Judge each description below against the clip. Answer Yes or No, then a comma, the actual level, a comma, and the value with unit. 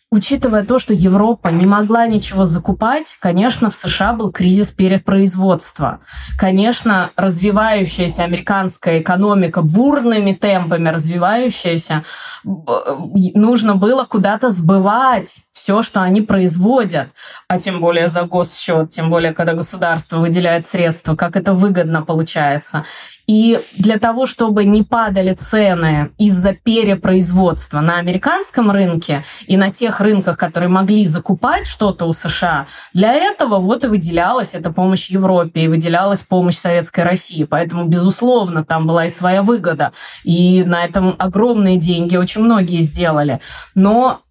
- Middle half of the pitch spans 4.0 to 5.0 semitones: No, average, 3.5 semitones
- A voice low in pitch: No, high, 190 Hz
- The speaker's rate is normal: Yes, average, 130 wpm